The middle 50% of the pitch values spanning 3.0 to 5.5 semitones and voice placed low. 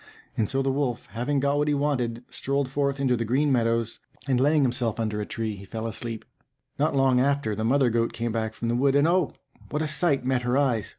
Yes: average, 3.5 semitones; low, 130 Hz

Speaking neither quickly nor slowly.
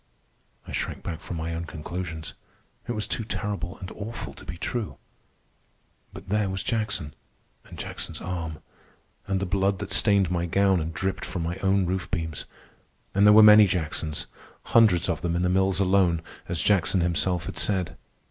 Yes: average, 175 wpm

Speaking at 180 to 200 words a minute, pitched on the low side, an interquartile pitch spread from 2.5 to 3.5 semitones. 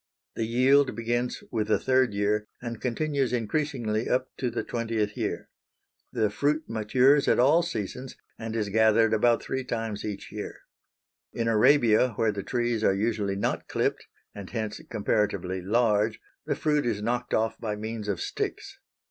No: average, 160 wpm; low, 115 Hz; average, 2.9 semitones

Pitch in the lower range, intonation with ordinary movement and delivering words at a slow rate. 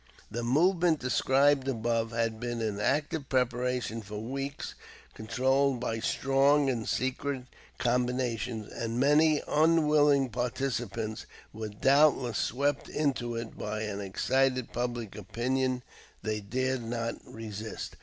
Yes: low, 125 Hz; average, 3.2 semitones; slow, 115 wpm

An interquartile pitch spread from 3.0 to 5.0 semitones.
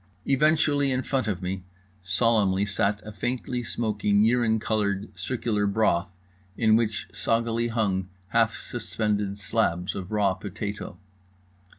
No: narrow, 2.6 semitones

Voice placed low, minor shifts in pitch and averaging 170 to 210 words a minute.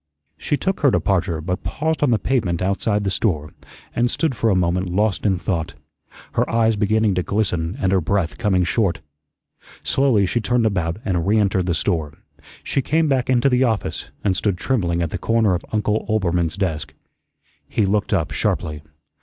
No: low, 100 Hz; average, 4.4 semitones; average, 180 wpm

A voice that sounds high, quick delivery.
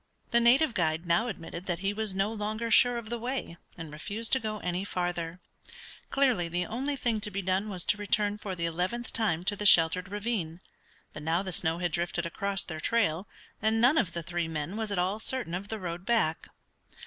Yes: high, 195 Hz; fast, 215 wpm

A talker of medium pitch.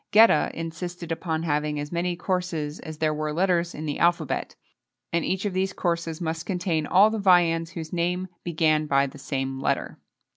Yes: medium, 165 Hz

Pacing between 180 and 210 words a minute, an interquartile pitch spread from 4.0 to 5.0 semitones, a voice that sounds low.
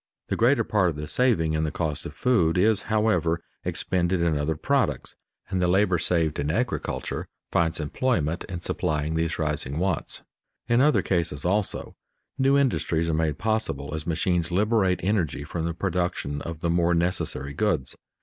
No: average, 170 wpm; average, 4.4 semitones; very low, 85 Hz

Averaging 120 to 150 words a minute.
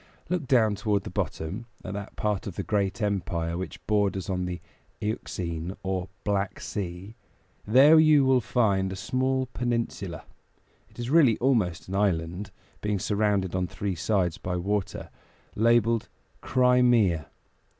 Yes: average, 140 wpm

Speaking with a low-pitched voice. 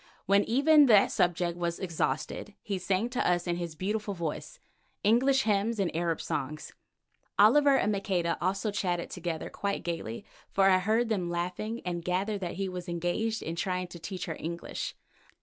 No: medium, 185 Hz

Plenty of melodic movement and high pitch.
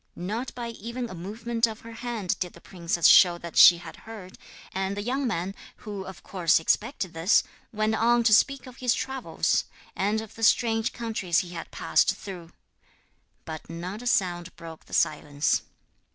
No: average, 4.8 semitones; high, 205 Hz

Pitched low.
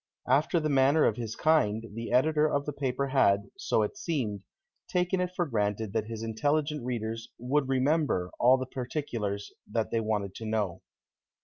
Yes: low, 125 Hz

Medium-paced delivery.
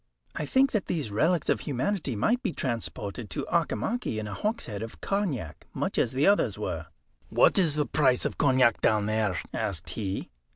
Yes: average, 180 wpm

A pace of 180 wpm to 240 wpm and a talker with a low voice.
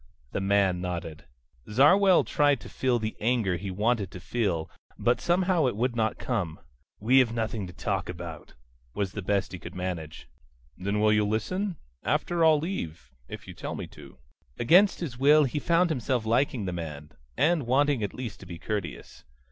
Yes: average, 185 wpm; low, 110 Hz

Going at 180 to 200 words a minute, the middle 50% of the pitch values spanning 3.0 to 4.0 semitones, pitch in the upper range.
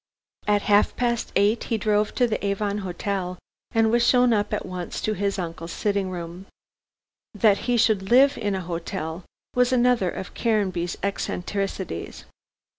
No: average, 155 wpm; average, 3.4 semitones; high, 200 Hz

